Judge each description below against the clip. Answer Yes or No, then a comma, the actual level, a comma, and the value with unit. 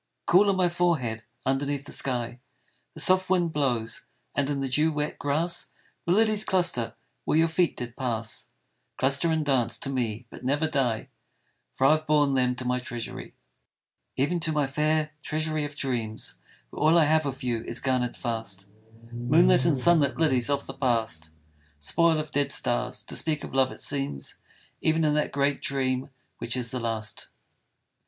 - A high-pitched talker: No, medium, 140 Hz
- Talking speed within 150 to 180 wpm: Yes, average, 175 wpm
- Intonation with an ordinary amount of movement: Yes, average, 4.1 semitones